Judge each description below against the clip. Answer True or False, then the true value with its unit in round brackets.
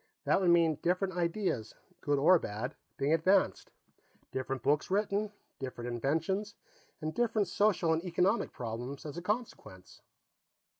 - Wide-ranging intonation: True (6.2 semitones)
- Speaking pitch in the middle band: True (165 Hz)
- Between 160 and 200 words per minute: False (135 wpm)